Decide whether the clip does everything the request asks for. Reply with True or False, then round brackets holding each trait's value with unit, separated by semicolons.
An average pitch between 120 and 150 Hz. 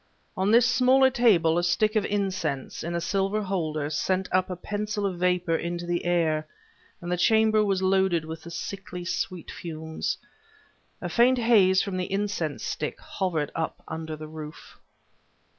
False (185 Hz)